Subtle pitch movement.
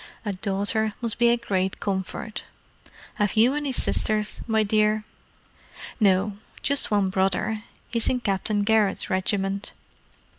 Yes: narrow, 2.2 semitones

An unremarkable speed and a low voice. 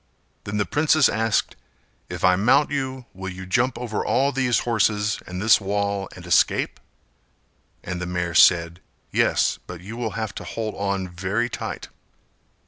Yes: average, 160 wpm; low, 105 Hz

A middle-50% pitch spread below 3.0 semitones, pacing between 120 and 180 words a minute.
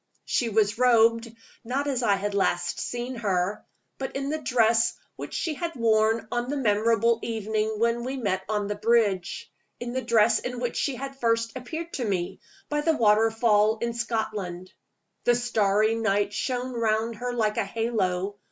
Yes: narrow, 2.6 semitones; average, 170 wpm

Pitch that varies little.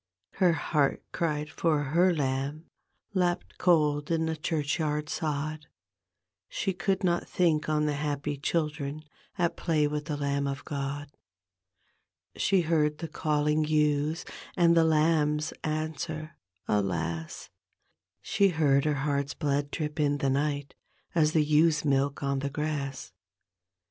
Yes: narrow, 2.0 semitones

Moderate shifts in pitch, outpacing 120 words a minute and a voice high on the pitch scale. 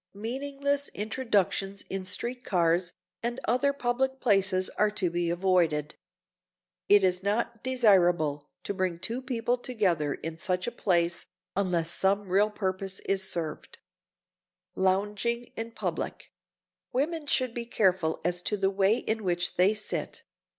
Yes: average, 4.7 semitones; average, 140 wpm; high, 195 Hz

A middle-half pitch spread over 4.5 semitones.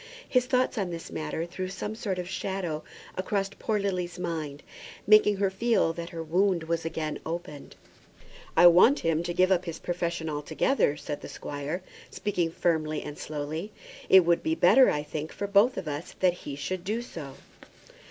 No: average, 3.6 semitones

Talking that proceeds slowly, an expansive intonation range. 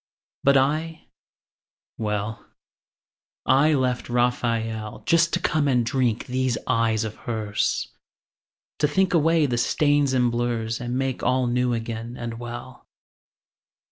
No: slow, 120 wpm; average, 3.2 semitones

